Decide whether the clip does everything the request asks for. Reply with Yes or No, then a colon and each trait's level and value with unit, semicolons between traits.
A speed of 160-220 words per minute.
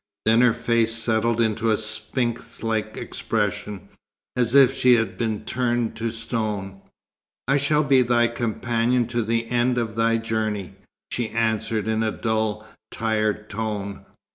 No: average, 145 wpm